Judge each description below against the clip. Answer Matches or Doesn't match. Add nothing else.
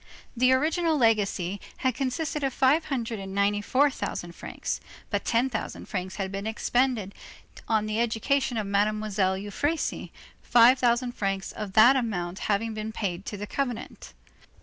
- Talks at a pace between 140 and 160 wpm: Matches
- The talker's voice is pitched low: Doesn't match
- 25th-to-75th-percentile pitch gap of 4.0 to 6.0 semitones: Matches